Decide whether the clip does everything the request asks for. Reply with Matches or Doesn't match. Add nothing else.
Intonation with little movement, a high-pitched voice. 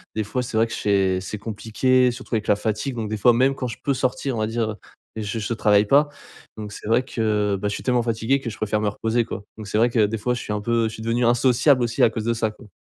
Doesn't match